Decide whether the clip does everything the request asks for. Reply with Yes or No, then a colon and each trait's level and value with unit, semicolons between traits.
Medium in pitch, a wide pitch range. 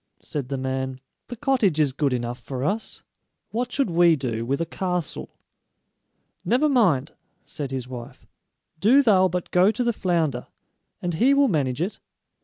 Yes: medium, 165 Hz; wide, 8.7 semitones